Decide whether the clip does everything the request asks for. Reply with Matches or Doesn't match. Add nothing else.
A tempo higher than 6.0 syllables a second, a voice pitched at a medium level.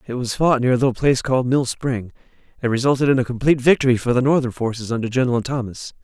Doesn't match